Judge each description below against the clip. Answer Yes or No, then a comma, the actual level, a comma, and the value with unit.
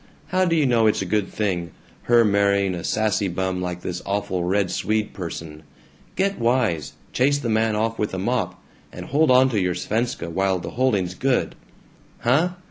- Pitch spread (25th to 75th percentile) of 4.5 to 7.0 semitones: Yes, average, 4.9 semitones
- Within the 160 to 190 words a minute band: Yes, average, 180 wpm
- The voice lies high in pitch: No, low, 105 Hz